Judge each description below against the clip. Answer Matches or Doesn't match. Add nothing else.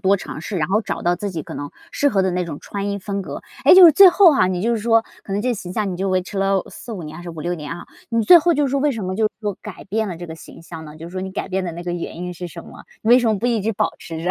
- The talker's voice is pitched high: Matches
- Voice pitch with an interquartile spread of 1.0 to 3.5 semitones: Doesn't match